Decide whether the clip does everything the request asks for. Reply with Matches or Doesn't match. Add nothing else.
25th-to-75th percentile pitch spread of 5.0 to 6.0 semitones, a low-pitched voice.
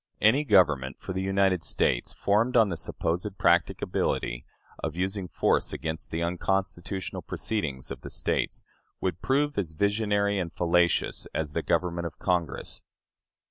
Doesn't match